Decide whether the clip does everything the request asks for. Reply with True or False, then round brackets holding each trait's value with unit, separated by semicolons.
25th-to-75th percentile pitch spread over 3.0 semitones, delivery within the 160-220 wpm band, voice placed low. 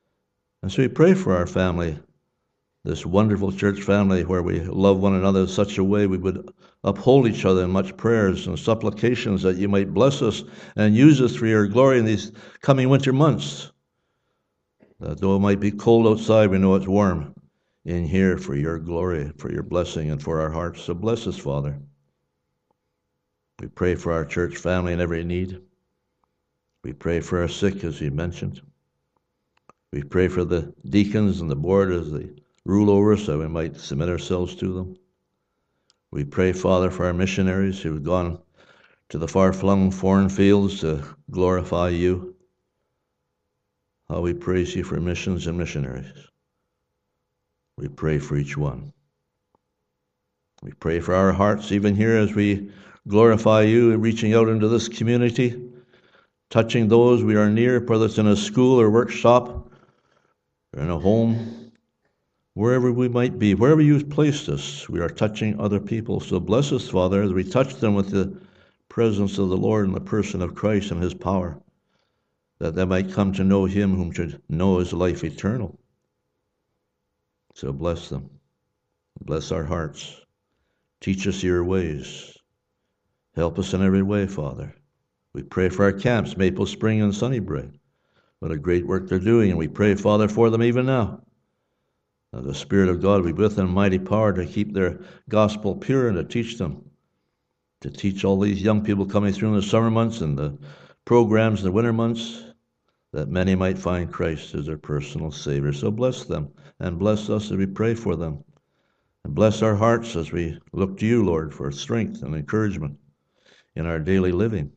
True (4.2 semitones; 175 wpm; 95 Hz)